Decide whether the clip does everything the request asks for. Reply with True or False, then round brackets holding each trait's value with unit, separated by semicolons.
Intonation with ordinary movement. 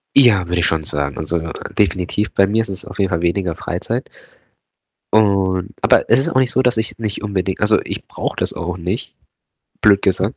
True (3.5 semitones)